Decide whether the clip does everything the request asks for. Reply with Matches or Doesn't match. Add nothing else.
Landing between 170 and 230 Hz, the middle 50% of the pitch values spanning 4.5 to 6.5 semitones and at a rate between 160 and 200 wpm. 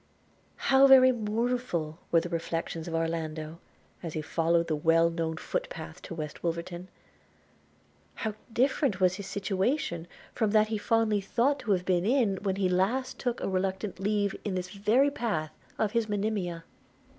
Matches